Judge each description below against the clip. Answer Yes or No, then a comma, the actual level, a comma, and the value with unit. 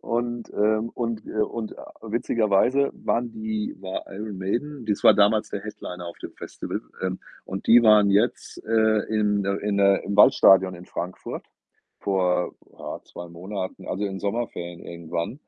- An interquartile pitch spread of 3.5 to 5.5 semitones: No, average, 2.7 semitones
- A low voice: Yes, low, 105 Hz